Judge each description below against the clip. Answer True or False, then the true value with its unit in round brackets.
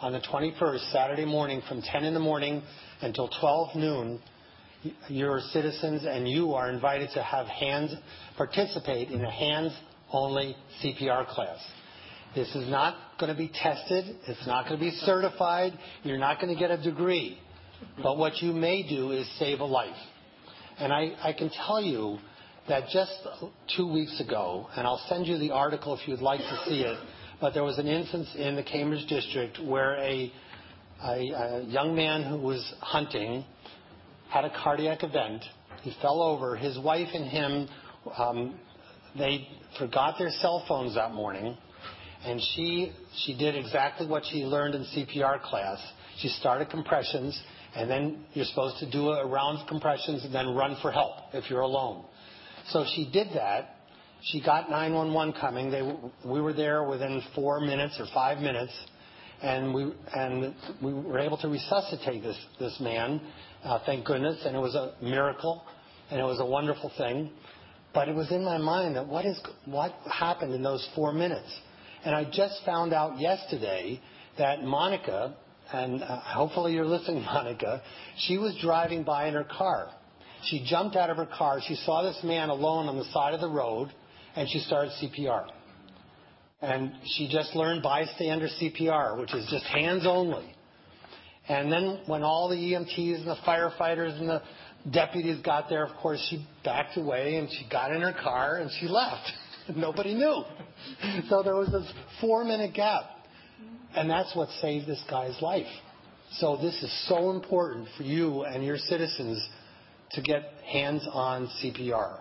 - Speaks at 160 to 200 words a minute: True (170 wpm)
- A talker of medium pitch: True (150 Hz)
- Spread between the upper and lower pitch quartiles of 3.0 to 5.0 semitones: True (3.7 semitones)